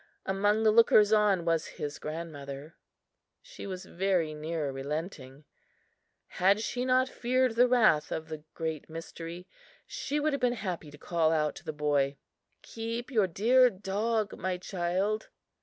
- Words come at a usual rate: Yes, average, 150 wpm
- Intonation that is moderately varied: No, wide, 5.9 semitones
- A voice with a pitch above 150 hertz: Yes, medium, 185 Hz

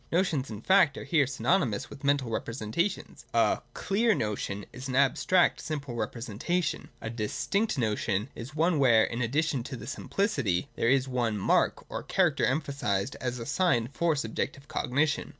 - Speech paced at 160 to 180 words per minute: Yes, average, 170 wpm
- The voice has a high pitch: No, low, 135 Hz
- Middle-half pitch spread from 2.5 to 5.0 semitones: No, wide, 5.4 semitones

